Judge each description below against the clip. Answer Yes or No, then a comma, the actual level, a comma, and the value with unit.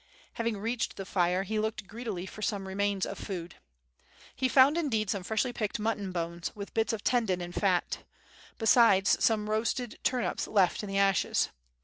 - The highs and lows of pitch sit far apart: No, average, 3.0 semitones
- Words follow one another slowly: No, average, 170 wpm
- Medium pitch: No, high, 210 Hz